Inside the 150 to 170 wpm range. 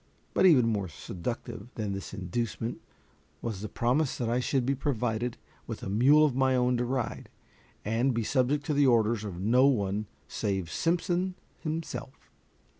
Yes: average, 165 wpm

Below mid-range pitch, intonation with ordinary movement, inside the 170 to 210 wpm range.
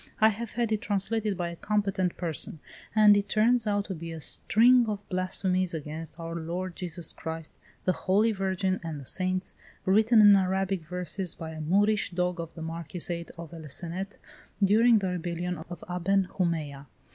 No: medium, 185 Hz; average, 3.4 semitones; average, 175 wpm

